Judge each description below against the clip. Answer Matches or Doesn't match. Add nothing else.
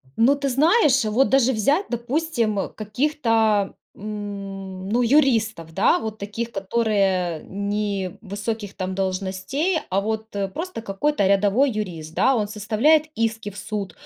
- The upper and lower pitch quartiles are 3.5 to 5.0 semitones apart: Matches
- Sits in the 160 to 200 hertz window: Doesn't match